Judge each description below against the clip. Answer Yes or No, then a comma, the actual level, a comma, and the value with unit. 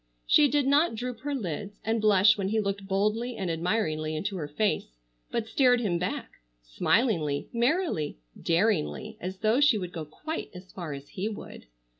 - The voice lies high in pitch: Yes, high, 205 Hz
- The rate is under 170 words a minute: No, average, 175 wpm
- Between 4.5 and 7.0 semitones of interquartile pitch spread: Yes, average, 5.2 semitones